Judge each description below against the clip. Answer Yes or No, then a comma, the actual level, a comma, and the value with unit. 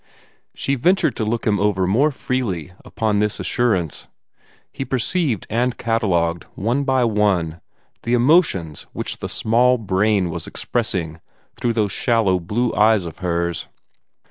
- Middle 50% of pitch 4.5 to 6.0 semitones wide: Yes, average, 5.0 semitones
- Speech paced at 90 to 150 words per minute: Yes, average, 140 wpm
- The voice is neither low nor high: No, low, 110 Hz